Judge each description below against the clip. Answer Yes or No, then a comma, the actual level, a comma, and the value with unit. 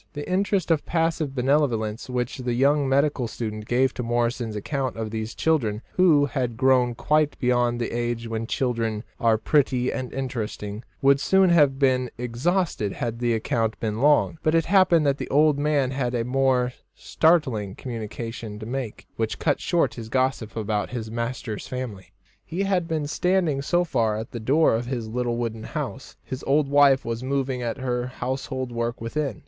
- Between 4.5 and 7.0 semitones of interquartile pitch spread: No, average, 3.8 semitones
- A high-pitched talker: No, low, 125 Hz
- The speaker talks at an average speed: Yes, average, 175 wpm